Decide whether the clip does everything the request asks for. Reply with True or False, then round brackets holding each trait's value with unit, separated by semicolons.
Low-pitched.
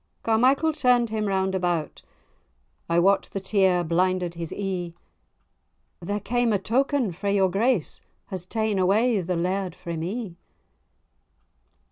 False (195 Hz)